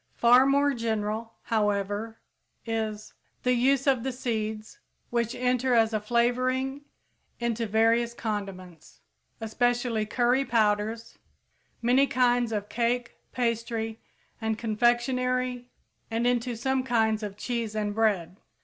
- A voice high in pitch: Yes, high, 230 Hz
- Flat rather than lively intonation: Yes, narrow, 2.2 semitones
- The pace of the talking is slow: Yes, slow, 115 wpm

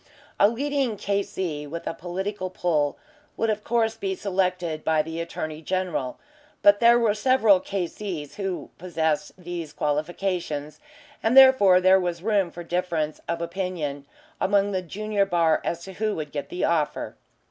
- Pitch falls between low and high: Yes, medium, 180 Hz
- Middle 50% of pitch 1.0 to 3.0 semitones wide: No, average, 3.9 semitones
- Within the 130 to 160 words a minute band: Yes, average, 155 wpm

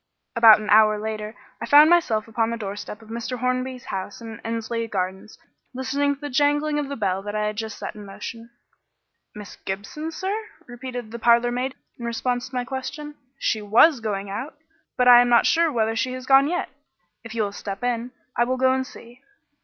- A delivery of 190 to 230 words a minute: Yes, average, 200 wpm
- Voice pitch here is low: No, high, 235 Hz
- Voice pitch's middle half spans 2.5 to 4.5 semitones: Yes, average, 3.3 semitones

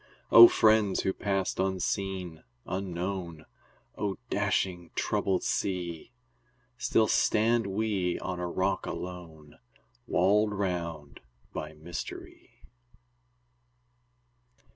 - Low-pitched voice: Yes, very low, 95 Hz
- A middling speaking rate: No, slow, 85 wpm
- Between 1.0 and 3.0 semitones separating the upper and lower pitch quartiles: Yes, narrow, 2.4 semitones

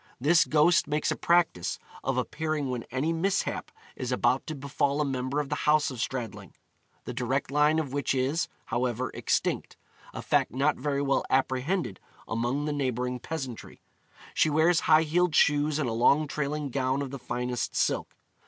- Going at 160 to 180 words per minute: Yes, average, 170 wpm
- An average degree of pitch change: Yes, average, 3.2 semitones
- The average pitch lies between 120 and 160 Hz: Yes, medium, 140 Hz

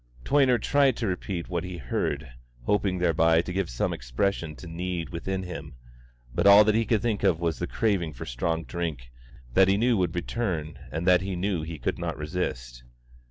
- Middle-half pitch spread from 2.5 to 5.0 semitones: Yes, average, 3.5 semitones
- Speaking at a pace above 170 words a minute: Yes, average, 200 wpm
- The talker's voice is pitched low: Yes, very low, 90 Hz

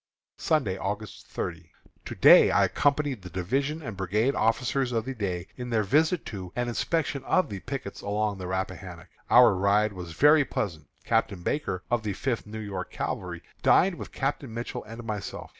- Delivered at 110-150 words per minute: No, average, 175 wpm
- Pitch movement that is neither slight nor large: No, wide, 6.0 semitones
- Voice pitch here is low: Yes, low, 110 Hz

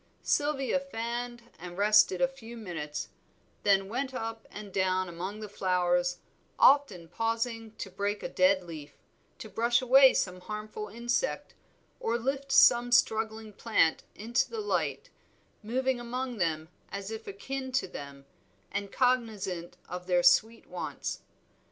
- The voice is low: No, high, 220 Hz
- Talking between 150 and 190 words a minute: No, average, 140 wpm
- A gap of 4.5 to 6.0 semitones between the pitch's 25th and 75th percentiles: Yes, average, 4.8 semitones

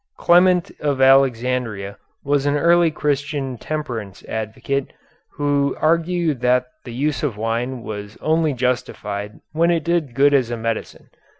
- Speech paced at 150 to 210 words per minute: No, slow, 135 wpm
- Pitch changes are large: No, average, 4.5 semitones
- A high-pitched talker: No, low, 135 Hz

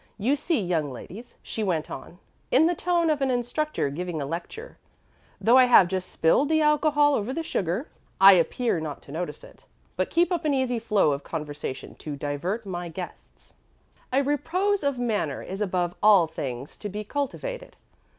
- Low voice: No, high, 215 Hz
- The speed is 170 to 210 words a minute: Yes, average, 180 wpm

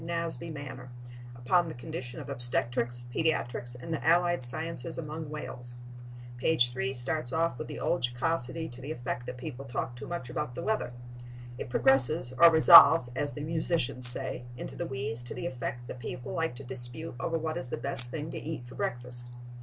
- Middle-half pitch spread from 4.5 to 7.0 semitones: Yes, average, 4.8 semitones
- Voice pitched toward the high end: No, low, 130 Hz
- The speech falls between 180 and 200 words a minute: Yes, average, 190 wpm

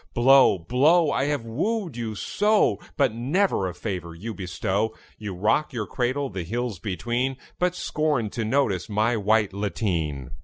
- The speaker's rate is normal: Yes, average, 155 wpm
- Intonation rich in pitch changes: Yes, wide, 5.8 semitones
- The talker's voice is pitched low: Yes, low, 115 Hz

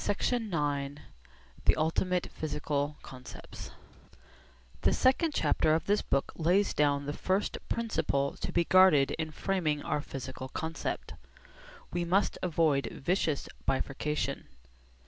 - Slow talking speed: Yes, slow, 120 wpm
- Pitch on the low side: No, medium, 155 Hz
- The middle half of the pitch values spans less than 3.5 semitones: No, average, 4.4 semitones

